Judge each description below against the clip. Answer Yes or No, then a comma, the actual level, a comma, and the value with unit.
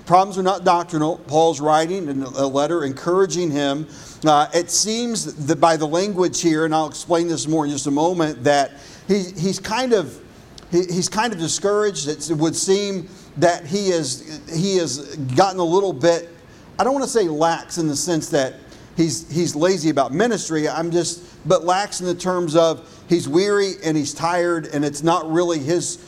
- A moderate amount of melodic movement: Yes, average, 3.1 semitones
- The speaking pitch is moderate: Yes, medium, 165 Hz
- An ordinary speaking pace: Yes, average, 195 wpm